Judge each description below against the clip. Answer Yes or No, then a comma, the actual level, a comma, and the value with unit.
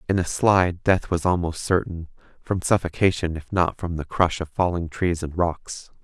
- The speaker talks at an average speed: Yes, average, 190 wpm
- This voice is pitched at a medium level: No, very low, 85 Hz